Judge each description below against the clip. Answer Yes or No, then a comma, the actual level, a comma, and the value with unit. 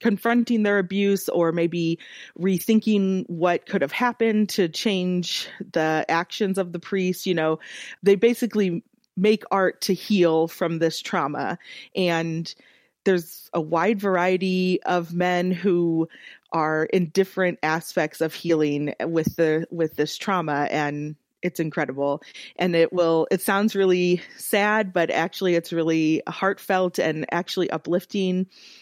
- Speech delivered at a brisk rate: No, slow, 135 wpm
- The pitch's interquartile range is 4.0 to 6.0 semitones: No, average, 2.9 semitones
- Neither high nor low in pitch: Yes, medium, 180 Hz